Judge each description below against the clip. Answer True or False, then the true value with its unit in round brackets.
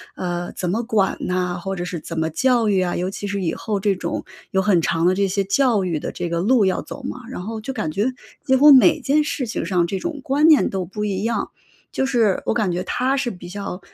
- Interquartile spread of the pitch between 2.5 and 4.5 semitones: False (5.1 semitones)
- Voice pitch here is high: True (200 Hz)